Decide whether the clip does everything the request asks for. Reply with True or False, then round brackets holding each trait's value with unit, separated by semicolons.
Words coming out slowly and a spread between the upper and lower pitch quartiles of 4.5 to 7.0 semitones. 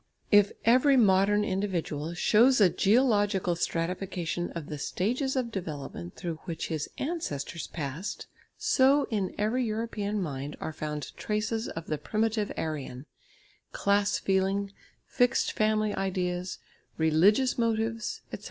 True (125 wpm; 5.0 semitones)